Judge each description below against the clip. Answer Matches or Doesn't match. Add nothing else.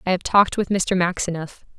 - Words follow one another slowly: Doesn't match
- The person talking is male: Doesn't match